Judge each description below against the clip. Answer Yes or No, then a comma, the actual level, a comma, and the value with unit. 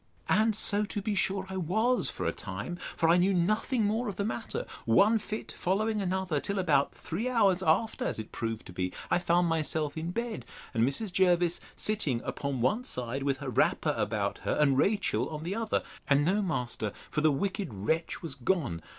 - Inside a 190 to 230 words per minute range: Yes, average, 200 wpm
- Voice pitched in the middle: Yes, medium, 175 Hz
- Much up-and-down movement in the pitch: Yes, wide, 6.6 semitones